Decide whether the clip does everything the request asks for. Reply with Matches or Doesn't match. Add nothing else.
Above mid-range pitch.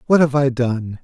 Doesn't match